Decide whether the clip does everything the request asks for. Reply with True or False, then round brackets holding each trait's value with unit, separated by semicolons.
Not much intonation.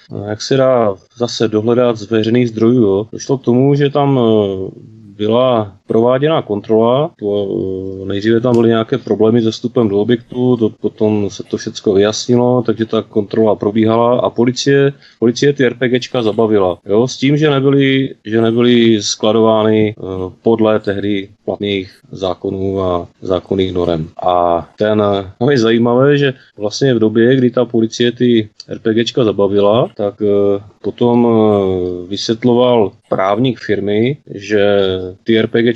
False (3.2 semitones)